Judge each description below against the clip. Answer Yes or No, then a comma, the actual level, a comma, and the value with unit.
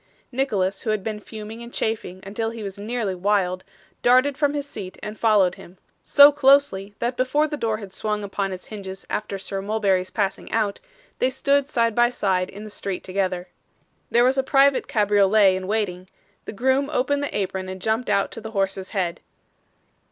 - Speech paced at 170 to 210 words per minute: Yes, average, 190 wpm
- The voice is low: No, high, 210 Hz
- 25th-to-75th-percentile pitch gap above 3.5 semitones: Yes, average, 4.1 semitones